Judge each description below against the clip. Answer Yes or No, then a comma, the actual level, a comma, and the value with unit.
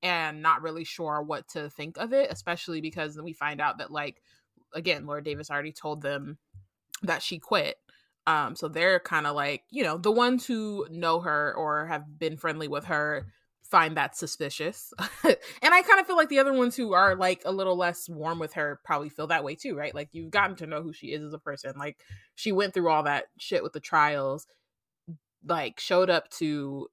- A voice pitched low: No, medium, 155 Hz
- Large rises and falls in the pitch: No, average, 3.4 semitones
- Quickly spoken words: Yes, fast, 215 wpm